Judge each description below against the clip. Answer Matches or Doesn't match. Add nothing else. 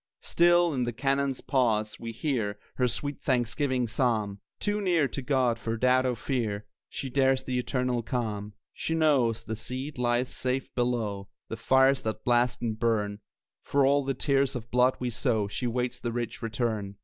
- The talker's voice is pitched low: Matches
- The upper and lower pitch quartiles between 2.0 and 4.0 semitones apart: Matches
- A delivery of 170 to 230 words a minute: Matches